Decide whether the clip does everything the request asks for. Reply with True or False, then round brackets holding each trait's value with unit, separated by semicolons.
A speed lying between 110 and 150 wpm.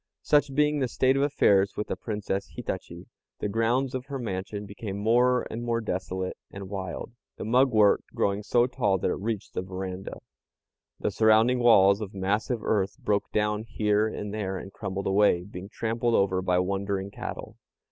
False (175 wpm)